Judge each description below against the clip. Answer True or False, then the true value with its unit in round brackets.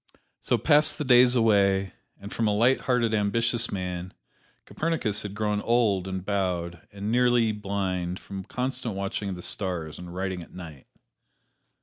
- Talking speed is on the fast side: False (155 wpm)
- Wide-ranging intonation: False (3.9 semitones)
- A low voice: True (100 Hz)